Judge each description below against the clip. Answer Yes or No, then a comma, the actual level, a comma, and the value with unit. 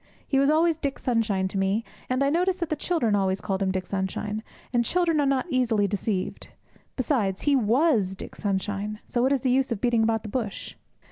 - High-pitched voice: Yes, high, 230 Hz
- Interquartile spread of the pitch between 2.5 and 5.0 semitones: No, wide, 5.5 semitones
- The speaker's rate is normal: No, fast, 210 wpm